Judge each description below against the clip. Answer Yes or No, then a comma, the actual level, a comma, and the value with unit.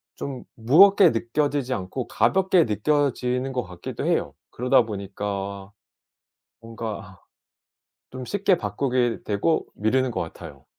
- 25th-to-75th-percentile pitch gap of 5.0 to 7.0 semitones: Yes, wide, 5.4 semitones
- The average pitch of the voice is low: Yes, low, 120 Hz